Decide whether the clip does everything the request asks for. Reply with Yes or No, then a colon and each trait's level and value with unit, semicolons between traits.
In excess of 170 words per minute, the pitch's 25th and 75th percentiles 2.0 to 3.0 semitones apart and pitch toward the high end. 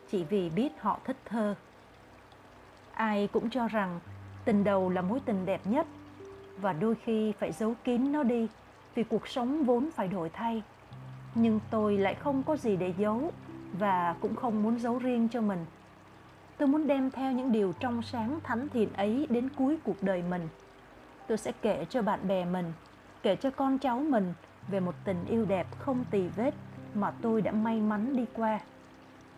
No: average, 185 wpm; average, 4.4 semitones; high, 215 Hz